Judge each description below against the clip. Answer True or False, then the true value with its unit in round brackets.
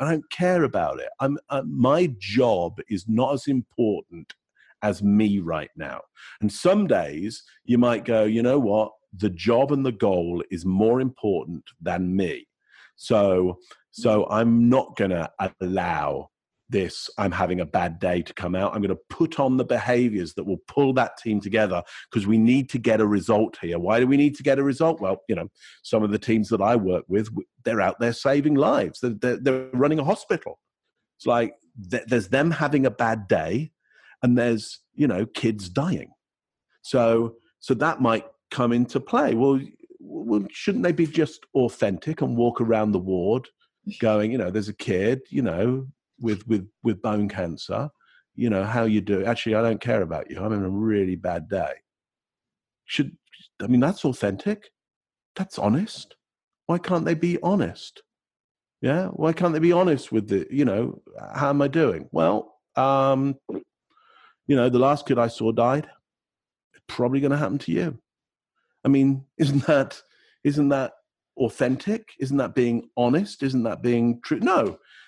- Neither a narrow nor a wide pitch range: True (4.7 semitones)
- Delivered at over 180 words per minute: False (175 wpm)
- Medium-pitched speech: False (125 Hz)